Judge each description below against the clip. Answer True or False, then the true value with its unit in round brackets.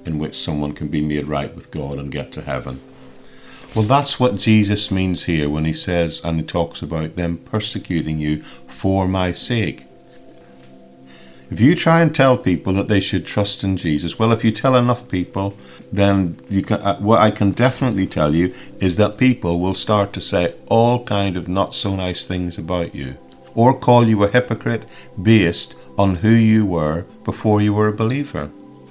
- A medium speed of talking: True (190 wpm)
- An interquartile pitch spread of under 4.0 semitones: False (4.8 semitones)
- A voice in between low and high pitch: False (95 Hz)